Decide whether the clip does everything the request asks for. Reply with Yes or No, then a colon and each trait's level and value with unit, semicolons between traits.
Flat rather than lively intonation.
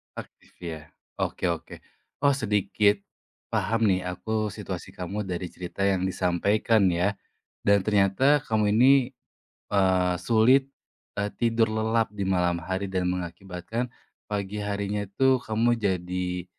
No: average, 3.3 semitones